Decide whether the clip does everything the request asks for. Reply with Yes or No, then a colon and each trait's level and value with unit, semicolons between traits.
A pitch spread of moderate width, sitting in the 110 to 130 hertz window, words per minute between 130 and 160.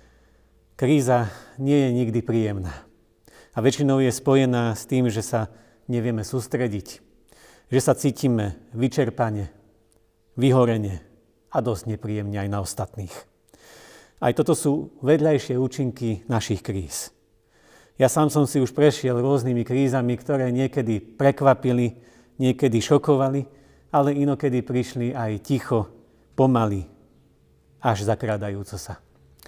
No: average, 3.8 semitones; low, 120 Hz; slow, 110 wpm